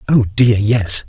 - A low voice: Yes, low, 110 Hz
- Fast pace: No, average, 165 wpm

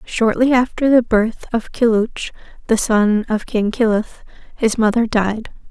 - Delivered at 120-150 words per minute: Yes, average, 145 wpm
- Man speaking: No, female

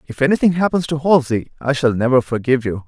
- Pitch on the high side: No, medium, 140 Hz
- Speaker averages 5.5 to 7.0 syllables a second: Yes, 6.5 syllables/s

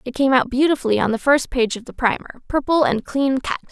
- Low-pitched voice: No, very high, 260 Hz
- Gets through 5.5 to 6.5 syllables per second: Yes, 6.2 syllables/s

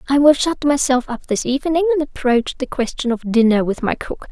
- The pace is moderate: No, fast, 225 wpm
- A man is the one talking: No, female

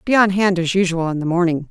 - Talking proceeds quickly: Yes, fast, 280 wpm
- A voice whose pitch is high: No, medium, 180 Hz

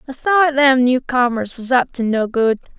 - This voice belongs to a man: No, female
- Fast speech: No, average, 195 wpm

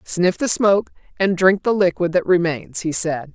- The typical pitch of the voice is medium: Yes, medium, 180 Hz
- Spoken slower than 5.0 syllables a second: Yes, 4.7 syllables/s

